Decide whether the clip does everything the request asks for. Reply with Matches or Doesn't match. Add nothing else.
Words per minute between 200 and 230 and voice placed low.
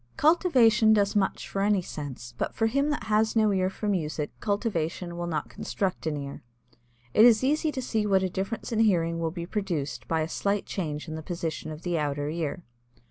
Doesn't match